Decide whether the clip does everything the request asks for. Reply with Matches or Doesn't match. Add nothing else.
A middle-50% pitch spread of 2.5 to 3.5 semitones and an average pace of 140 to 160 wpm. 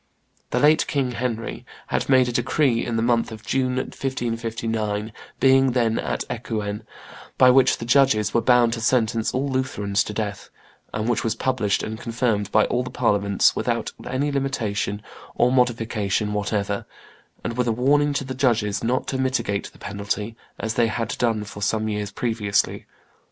Doesn't match